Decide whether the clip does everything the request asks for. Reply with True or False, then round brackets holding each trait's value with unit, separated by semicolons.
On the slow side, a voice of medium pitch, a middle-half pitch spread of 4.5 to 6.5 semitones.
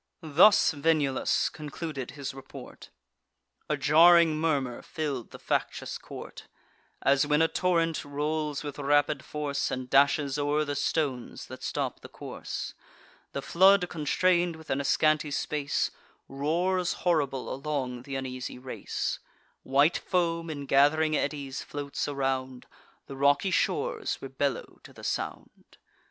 False (130 wpm; 145 Hz; 2.6 semitones)